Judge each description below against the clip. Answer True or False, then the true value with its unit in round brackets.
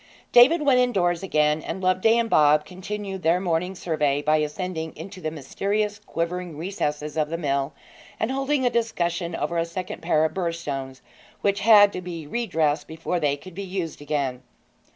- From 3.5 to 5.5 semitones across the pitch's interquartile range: True (4.4 semitones)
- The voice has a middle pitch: True (175 Hz)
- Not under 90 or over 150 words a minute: False (180 wpm)